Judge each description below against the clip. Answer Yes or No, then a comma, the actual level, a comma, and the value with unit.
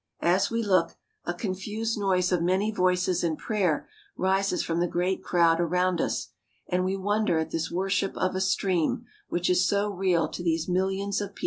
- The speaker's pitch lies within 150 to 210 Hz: Yes, medium, 185 Hz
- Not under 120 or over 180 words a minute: No, average, 190 wpm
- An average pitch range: No, narrow, 2.0 semitones